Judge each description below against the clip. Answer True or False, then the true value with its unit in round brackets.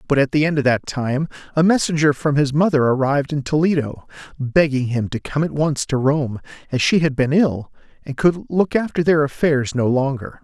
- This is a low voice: False (145 Hz)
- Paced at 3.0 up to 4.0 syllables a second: False (5.2 syllables/s)